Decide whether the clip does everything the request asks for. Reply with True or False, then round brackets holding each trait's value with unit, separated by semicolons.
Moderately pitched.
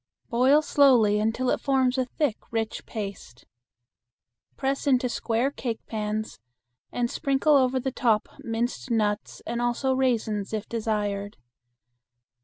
False (235 Hz)